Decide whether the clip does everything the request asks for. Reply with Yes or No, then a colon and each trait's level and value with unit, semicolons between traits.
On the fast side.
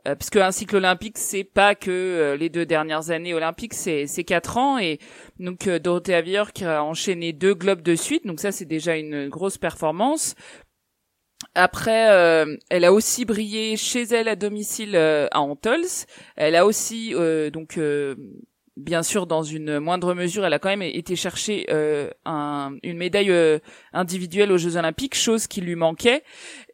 No: average, 185 wpm